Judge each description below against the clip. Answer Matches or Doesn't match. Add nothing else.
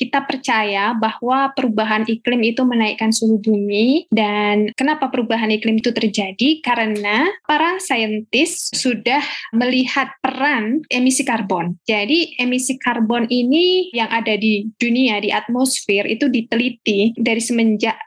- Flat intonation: Doesn't match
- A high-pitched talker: Matches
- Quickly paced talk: Doesn't match